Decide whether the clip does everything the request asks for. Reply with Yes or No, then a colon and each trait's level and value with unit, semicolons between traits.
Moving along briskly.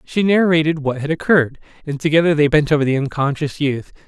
No: average, 190 wpm